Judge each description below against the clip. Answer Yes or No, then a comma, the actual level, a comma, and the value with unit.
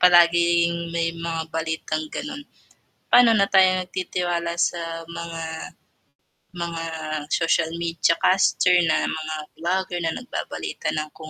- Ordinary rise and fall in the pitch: No, narrow, 1.5 semitones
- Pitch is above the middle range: No, medium, 170 Hz